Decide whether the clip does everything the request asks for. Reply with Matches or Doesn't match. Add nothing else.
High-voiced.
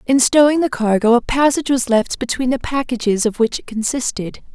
Matches